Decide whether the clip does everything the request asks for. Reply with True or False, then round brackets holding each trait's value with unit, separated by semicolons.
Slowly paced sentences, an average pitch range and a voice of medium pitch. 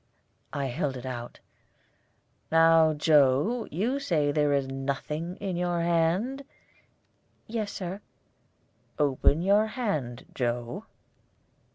False (105 wpm; 6.0 semitones; 160 Hz)